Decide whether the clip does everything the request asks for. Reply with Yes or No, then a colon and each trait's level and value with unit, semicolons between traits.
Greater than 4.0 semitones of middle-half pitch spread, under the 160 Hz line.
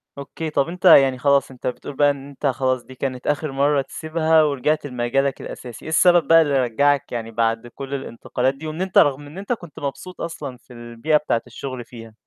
No: average, 3.4 semitones; medium, 140 Hz